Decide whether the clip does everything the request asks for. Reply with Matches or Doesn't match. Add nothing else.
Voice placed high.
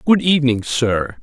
Doesn't match